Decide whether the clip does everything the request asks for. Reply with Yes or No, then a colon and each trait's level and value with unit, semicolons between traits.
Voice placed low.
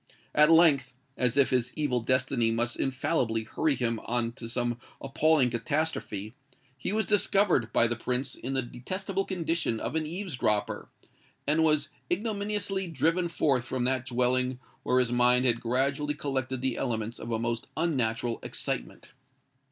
Yes: low, 130 Hz